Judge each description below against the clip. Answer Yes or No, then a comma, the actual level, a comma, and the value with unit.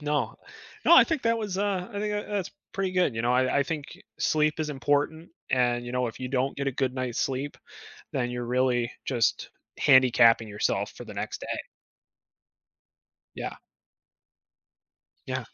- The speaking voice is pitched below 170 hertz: Yes, low, 135 Hz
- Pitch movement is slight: No, average, 4.8 semitones